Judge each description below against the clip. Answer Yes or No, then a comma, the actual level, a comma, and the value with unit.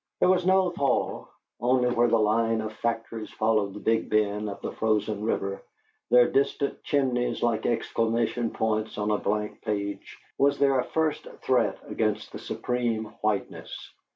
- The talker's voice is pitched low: Yes, low, 115 Hz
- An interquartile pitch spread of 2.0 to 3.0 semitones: Yes, narrow, 2.5 semitones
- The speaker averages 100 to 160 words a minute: Yes, average, 155 wpm